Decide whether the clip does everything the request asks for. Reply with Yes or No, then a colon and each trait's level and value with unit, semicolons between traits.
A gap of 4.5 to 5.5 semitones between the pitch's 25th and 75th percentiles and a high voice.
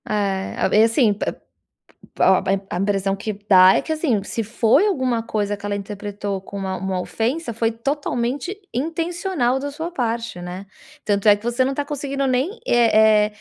Yes: average, 5.2 semitones; high, 225 Hz